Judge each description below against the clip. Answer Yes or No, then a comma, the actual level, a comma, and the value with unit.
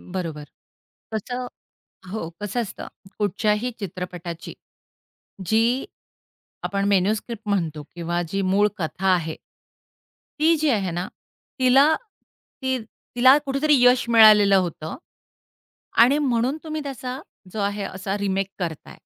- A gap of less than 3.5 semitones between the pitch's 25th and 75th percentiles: No, average, 5.2 semitones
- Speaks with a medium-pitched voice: No, high, 205 Hz